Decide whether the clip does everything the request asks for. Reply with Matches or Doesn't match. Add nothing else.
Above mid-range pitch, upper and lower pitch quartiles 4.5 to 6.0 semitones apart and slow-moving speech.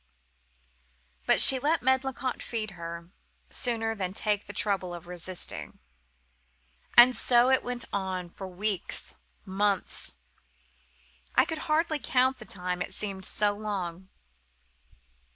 Matches